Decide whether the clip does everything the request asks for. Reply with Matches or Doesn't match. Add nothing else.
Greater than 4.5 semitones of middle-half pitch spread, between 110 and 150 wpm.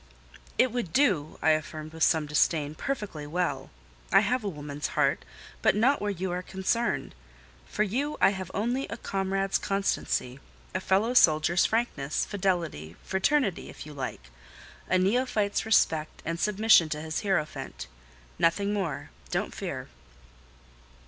Matches